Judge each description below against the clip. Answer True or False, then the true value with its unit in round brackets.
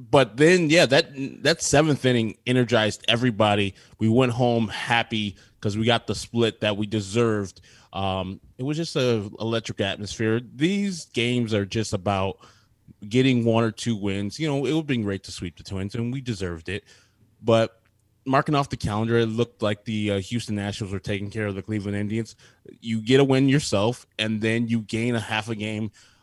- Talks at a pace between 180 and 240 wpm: True (195 wpm)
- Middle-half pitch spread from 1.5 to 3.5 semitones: True (2.9 semitones)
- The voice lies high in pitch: False (115 Hz)